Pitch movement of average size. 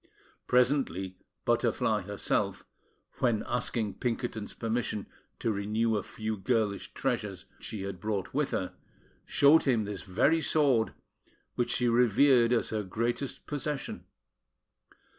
Yes: average, 3.3 semitones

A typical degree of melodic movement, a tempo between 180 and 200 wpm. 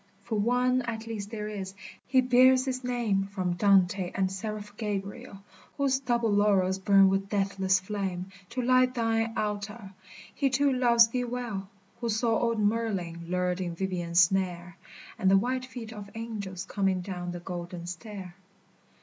No: average, 3.7 semitones; average, 170 wpm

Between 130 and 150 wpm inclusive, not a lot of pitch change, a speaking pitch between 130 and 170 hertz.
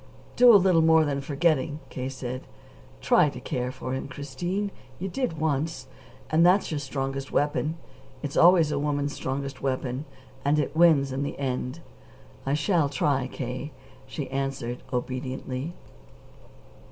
No: average, 145 wpm; average, 3.4 semitones; medium, 140 Hz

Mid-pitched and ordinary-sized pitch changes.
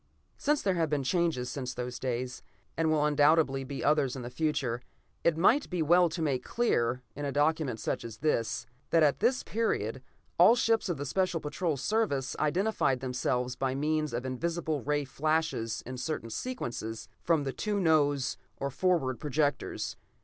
Yes: medium, 150 Hz; average, 4.5 semitones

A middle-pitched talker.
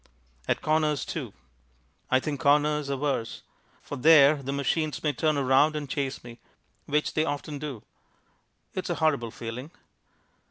Yes: medium, 145 Hz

